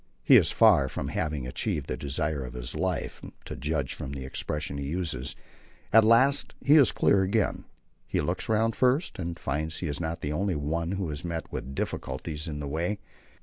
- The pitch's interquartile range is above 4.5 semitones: Yes, average, 4.9 semitones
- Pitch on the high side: No, very low, 80 Hz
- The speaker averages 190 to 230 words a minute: Yes, average, 195 wpm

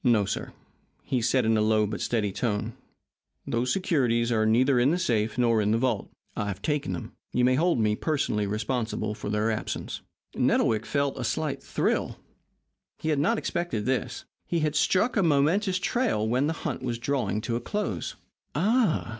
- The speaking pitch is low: Yes, low, 125 Hz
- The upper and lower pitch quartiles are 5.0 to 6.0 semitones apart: Yes, wide, 5.6 semitones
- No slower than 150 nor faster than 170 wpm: No, average, 185 wpm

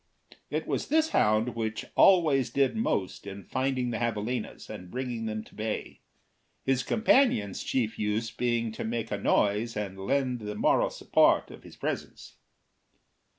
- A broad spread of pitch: No, average, 3.4 semitones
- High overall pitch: No, low, 115 Hz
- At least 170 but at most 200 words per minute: No, average, 150 wpm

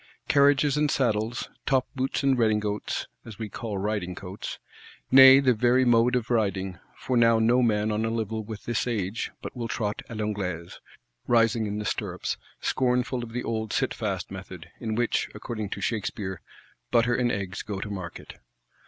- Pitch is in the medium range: No, low, 115 Hz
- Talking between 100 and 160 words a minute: No, average, 170 wpm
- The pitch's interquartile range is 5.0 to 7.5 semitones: No, average, 2.7 semitones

